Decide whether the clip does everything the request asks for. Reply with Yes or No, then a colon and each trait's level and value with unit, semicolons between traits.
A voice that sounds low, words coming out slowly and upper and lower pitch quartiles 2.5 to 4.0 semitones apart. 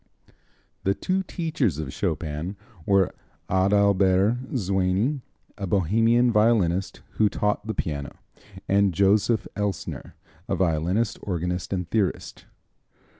Yes: low, 100 Hz; slow, 105 wpm; average, 3.1 semitones